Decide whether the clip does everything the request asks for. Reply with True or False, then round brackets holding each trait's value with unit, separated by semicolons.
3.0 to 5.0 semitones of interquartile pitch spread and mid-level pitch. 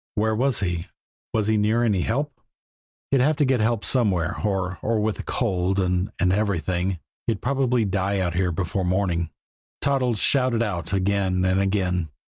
False (4.0 semitones; 100 Hz)